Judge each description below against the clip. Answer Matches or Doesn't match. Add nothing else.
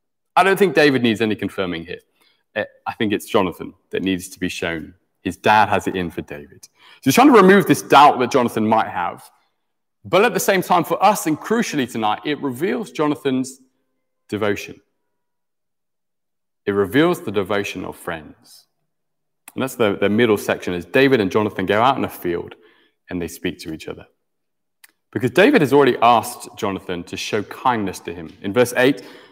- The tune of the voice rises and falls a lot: Matches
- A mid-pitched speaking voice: Doesn't match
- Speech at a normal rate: Matches